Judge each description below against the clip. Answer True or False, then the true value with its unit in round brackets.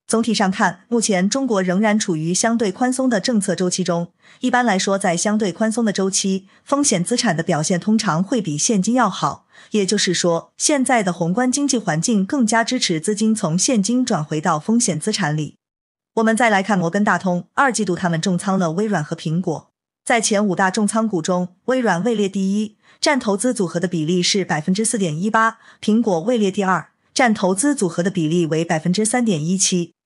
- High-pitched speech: True (200 Hz)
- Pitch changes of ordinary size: True (4.2 semitones)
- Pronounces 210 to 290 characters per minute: False (305 characters per minute)